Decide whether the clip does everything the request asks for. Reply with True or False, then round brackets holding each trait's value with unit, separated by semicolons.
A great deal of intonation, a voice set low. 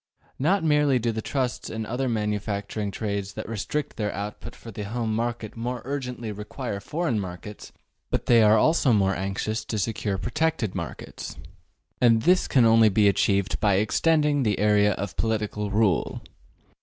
False (3.2 semitones; 110 Hz)